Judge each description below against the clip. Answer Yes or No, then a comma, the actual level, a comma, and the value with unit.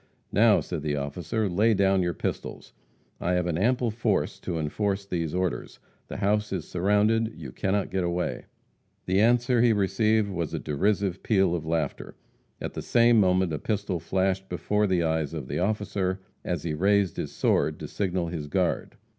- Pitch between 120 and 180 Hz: No, very low, 95 Hz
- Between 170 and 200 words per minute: Yes, average, 180 wpm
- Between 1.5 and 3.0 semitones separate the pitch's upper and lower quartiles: No, average, 3.5 semitones